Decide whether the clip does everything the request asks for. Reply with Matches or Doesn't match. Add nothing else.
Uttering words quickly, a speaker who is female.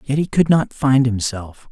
Doesn't match